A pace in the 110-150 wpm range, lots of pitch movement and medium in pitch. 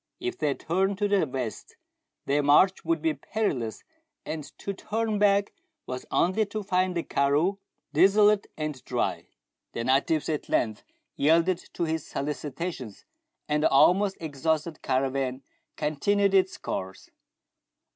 Yes: slow, 135 wpm; wide, 6.1 semitones; medium, 160 Hz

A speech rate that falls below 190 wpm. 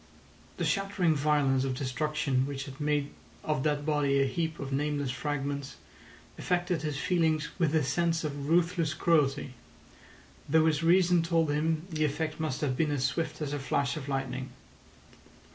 Yes: average, 160 wpm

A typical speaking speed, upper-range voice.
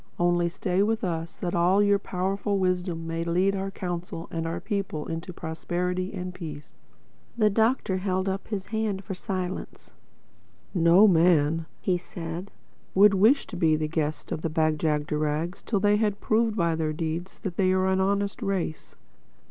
No: average, 170 wpm; medium, 180 Hz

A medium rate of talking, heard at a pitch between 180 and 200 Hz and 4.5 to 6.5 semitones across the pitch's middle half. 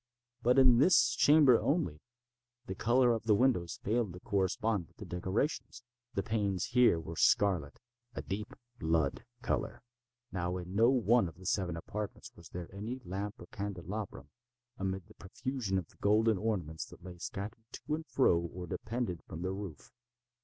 No: average, 160 wpm; low, 100 Hz; average, 4.8 semitones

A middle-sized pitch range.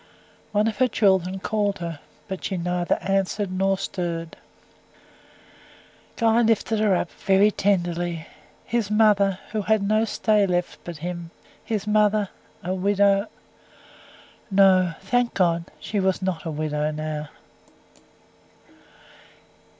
Yes: average, 3.1 semitones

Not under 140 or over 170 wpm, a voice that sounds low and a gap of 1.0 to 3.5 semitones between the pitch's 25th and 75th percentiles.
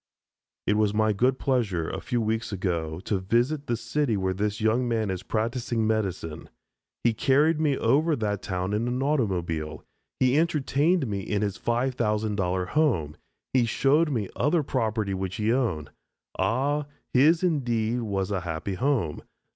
No: average, 155 wpm; low, 110 Hz; average, 5.3 semitones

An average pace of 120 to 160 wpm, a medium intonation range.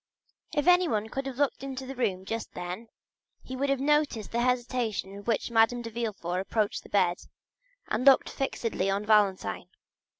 No: average, 170 wpm; average, 4.6 semitones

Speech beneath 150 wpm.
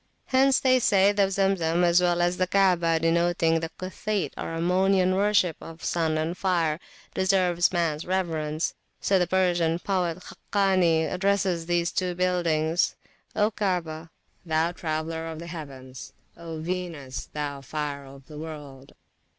Yes: average, 140 wpm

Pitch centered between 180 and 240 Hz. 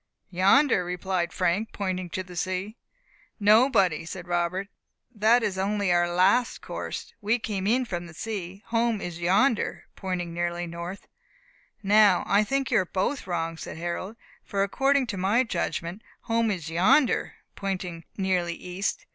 Yes: high, 190 Hz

